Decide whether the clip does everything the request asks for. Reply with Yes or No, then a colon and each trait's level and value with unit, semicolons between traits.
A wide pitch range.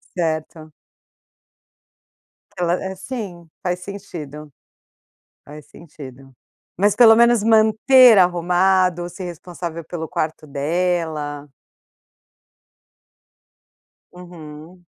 No: average, 3.4 semitones